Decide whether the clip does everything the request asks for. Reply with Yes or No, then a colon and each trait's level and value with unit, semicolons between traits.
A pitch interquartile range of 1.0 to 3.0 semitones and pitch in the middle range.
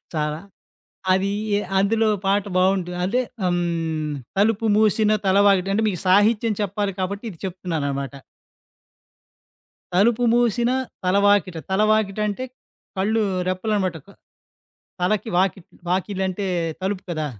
No: average, 2.7 semitones; high, 195 Hz